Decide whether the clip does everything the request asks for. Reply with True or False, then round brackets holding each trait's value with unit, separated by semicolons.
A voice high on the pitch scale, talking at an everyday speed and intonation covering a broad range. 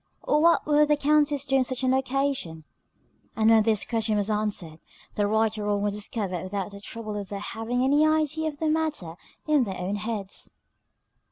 True (225 Hz; 195 wpm; 5.7 semitones)